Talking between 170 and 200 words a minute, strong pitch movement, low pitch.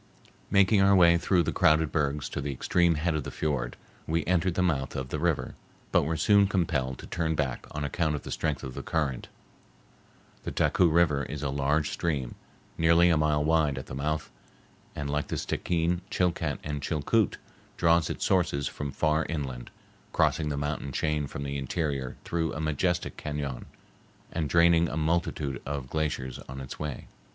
No: average, 180 wpm; average, 3.0 semitones; very low, 75 Hz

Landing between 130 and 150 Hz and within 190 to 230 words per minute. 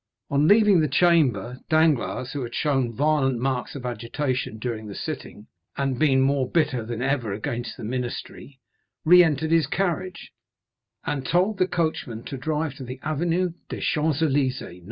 No: medium, 140 Hz; average, 165 wpm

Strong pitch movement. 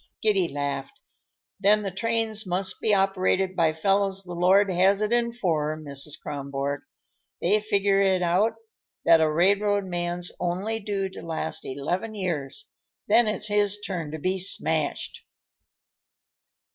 No: average, 3.6 semitones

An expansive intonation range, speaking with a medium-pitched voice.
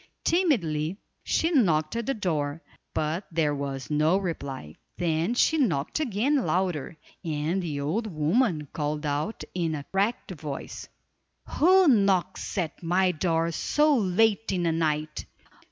Yes: wide, 5.7 semitones; medium, 170 Hz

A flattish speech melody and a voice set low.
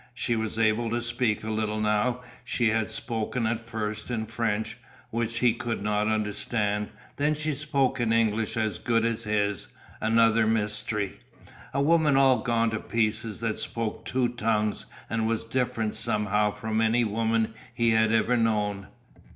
Yes: narrow, 1.6 semitones; low, 110 Hz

